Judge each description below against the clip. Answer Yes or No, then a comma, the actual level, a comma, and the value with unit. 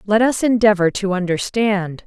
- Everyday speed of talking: Yes, average, 145 wpm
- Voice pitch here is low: No, high, 200 Hz